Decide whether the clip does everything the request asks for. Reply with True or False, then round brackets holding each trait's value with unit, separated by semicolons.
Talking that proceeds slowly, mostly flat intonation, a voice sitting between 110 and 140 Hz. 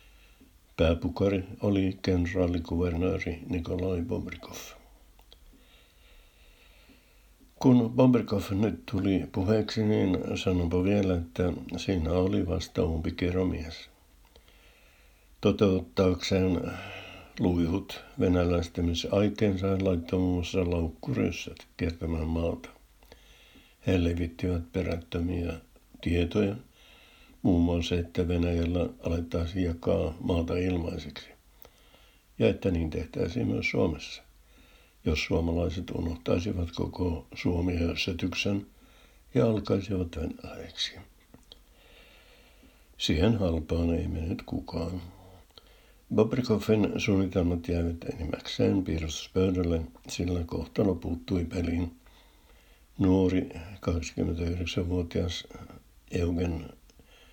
False (75 wpm; 2.1 semitones; 90 Hz)